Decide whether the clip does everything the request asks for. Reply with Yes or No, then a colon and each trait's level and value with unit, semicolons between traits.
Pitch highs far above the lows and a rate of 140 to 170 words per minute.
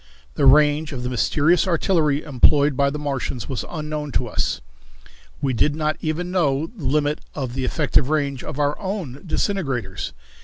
No: narrow, 2.6 semitones; average, 165 wpm